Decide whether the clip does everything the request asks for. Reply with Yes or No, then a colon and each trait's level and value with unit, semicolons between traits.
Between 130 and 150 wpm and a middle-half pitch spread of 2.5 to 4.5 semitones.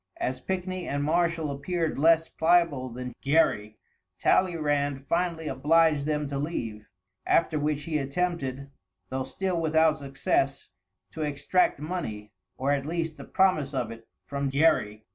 Yes: average, 140 wpm; average, 3.5 semitones